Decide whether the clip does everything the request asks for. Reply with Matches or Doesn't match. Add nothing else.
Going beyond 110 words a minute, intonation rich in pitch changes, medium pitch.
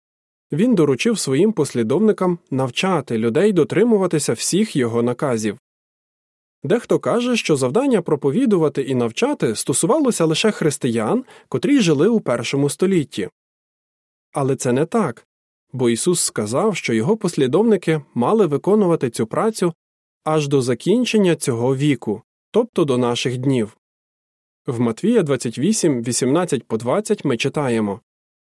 Matches